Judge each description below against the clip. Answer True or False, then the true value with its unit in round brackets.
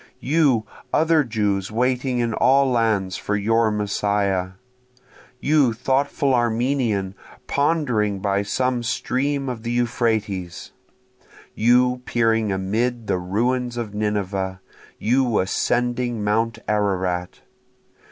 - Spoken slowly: True (105 wpm)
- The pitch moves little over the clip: False (3.6 semitones)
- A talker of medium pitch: False (115 Hz)